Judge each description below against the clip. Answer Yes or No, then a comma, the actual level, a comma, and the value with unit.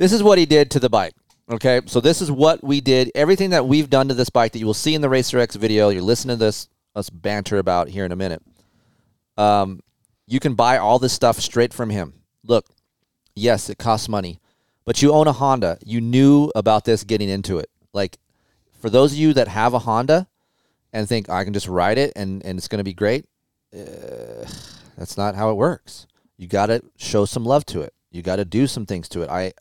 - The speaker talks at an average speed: No, fast, 235 wpm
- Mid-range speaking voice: No, low, 115 Hz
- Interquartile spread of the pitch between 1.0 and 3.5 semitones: No, average, 4.8 semitones